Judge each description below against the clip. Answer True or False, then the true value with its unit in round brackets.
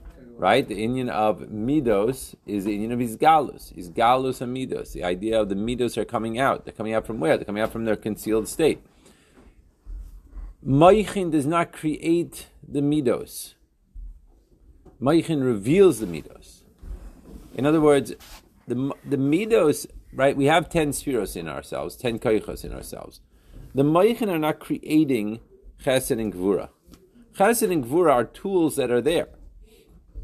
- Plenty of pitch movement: True (6.1 semitones)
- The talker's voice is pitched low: True (125 Hz)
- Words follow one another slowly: False (150 wpm)